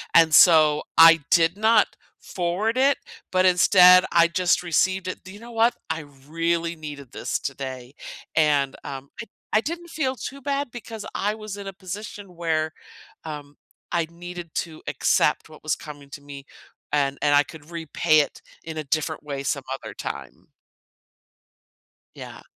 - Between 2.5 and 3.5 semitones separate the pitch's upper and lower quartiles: No, average, 4.7 semitones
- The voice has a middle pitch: Yes, medium, 170 Hz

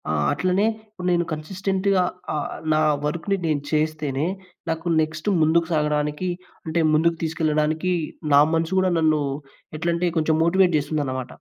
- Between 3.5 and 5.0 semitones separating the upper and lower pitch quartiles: No, average, 2.7 semitones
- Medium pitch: Yes, medium, 160 Hz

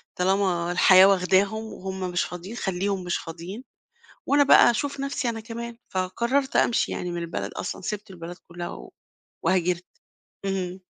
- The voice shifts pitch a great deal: No, average, 3.7 semitones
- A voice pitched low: No, high, 190 Hz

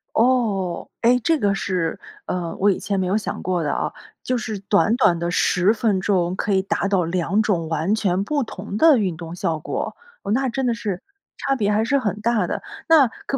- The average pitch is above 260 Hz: No, high, 200 Hz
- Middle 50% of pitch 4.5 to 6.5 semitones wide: No, average, 4.1 semitones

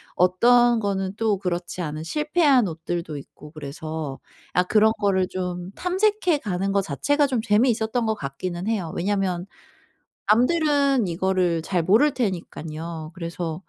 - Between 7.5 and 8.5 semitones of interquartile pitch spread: No, wide, 5.5 semitones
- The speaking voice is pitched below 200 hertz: Yes, high, 190 Hz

